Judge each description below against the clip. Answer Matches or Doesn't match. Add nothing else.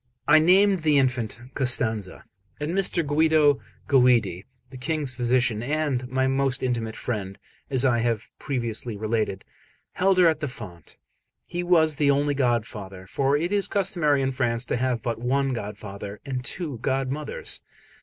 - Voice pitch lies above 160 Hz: Doesn't match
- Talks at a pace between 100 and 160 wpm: Matches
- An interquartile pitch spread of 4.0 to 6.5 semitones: Matches